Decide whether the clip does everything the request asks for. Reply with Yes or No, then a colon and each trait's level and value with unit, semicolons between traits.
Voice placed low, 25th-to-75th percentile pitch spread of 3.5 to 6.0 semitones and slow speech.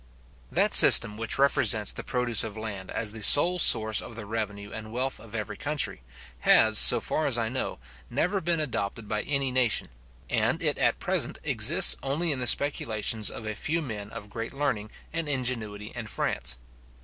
No: low, 115 Hz; average, 4.4 semitones; average, 185 wpm